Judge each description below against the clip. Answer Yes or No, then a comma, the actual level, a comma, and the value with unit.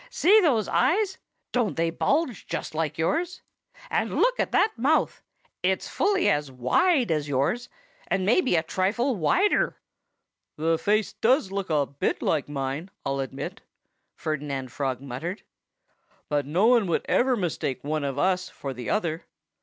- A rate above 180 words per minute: No, average, 155 wpm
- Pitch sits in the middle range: Yes, medium, 175 Hz